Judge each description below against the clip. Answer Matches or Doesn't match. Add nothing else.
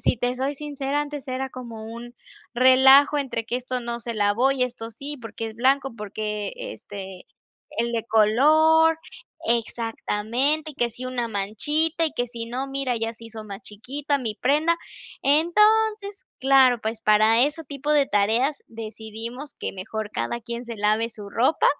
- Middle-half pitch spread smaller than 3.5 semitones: Doesn't match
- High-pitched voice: Matches